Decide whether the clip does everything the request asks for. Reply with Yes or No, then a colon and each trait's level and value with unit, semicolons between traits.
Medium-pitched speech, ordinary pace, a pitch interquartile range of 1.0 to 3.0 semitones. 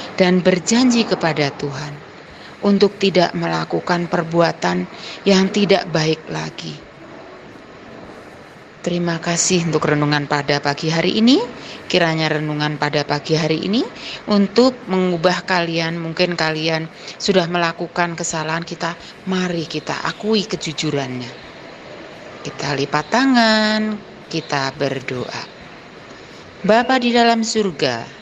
No: medium, 170 Hz; average, 100 wpm; average, 4.1 semitones